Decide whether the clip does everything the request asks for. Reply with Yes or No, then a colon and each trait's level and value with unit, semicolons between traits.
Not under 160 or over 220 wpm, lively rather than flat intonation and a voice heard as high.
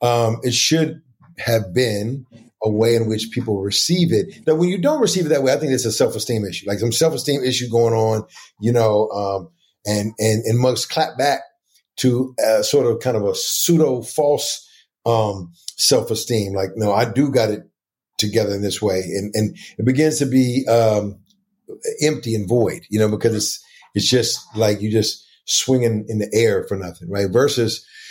No: average, 195 wpm; wide, 5.9 semitones; low, 115 Hz